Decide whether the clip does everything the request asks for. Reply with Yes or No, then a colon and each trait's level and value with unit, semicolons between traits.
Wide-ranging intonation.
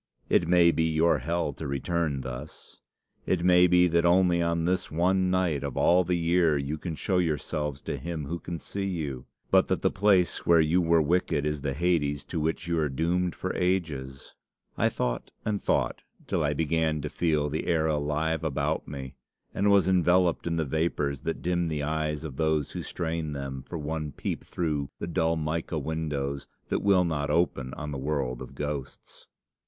No: average, 3.0 semitones